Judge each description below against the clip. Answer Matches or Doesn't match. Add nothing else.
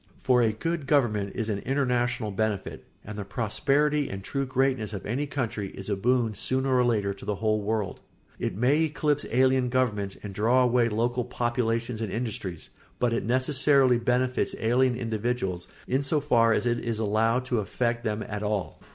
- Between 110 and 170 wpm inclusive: Doesn't match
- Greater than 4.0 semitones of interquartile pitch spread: Doesn't match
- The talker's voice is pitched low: Matches